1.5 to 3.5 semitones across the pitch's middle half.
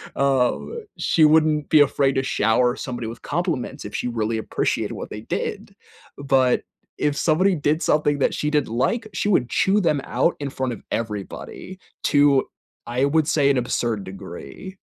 No: average, 4.2 semitones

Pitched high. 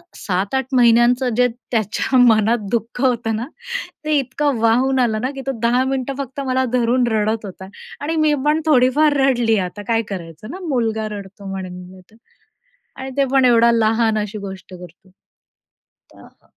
Yes: high, 235 Hz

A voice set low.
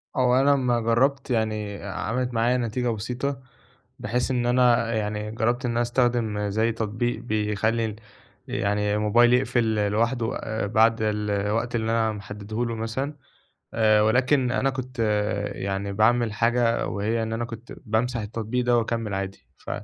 Yes: low, 115 Hz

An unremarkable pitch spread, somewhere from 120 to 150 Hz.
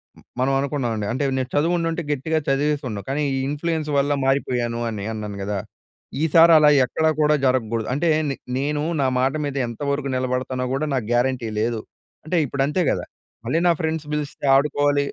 Yes: average, 3.1 semitones; medium, 140 Hz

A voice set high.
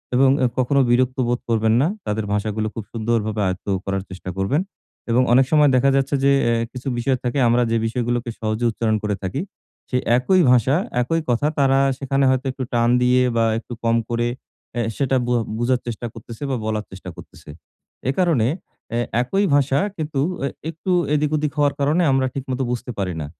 No: low, 125 Hz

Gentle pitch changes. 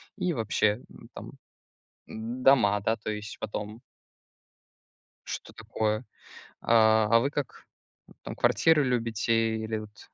Yes: narrow, 2.3 semitones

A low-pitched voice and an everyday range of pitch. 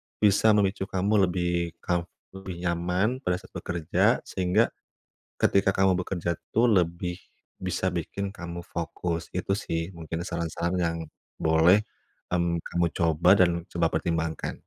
No: very low, 90 Hz; narrow, 2.0 semitones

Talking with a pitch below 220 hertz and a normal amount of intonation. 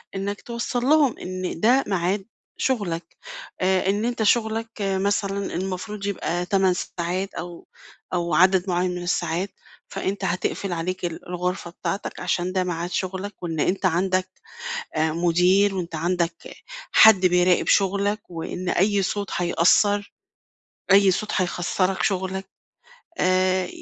No: medium, 185 Hz; narrow, 2.2 semitones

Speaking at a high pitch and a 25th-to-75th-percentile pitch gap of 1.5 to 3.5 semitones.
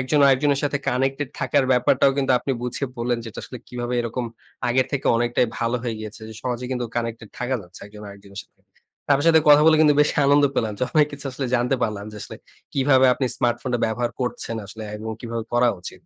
No: low, 125 Hz; average, 2.8 semitones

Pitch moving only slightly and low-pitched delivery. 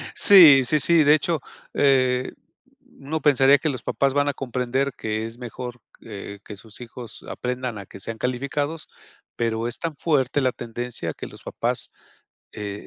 No: average, 3.5 semitones; low, 130 Hz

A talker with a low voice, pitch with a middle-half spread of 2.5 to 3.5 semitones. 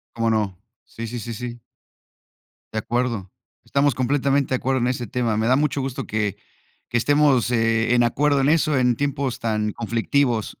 Yes: low, 120 Hz; average, 3.2 semitones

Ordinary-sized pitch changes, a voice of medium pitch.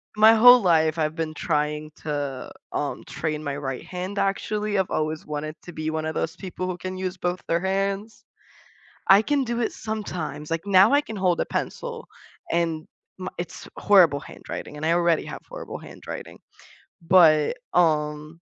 Yes: average, 4.0 semitones; medium, 170 Hz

